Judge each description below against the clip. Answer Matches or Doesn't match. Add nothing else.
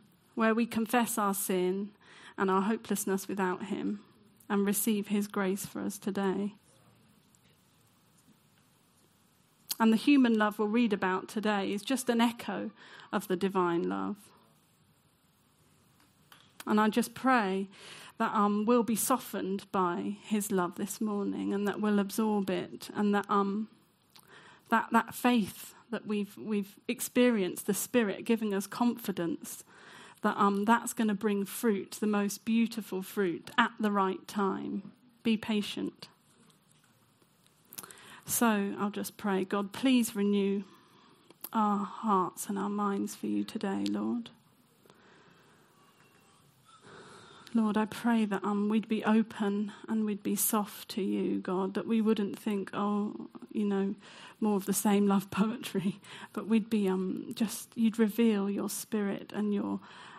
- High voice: Matches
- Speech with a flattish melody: Matches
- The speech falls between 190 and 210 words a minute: Doesn't match